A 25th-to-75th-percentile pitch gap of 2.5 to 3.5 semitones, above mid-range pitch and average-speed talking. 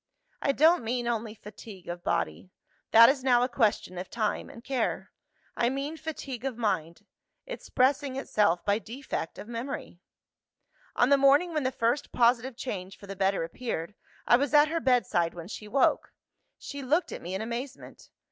No: average, 4.8 semitones; high, 240 Hz; average, 175 wpm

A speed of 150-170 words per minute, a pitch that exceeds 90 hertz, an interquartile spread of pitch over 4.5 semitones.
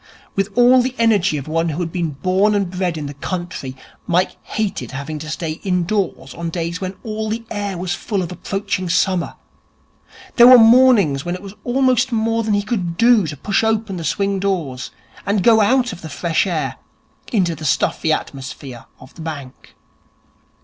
No: average, 185 wpm; medium, 185 Hz; average, 5.1 semitones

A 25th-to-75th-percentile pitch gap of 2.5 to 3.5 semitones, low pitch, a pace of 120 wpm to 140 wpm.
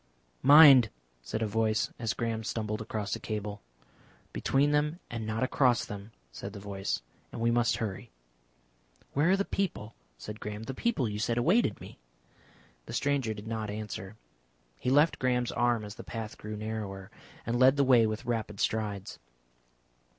No: average, 3.2 semitones; low, 110 Hz; average, 165 wpm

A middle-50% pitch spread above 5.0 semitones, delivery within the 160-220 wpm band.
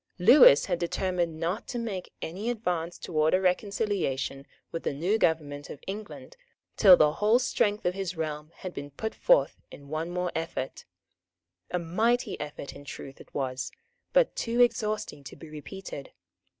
Yes: wide, 5.6 semitones; average, 165 wpm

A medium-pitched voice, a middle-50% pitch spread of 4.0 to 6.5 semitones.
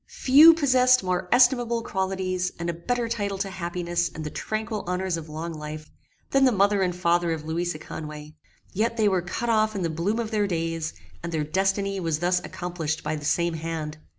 Yes: medium, 180 Hz; average, 4.5 semitones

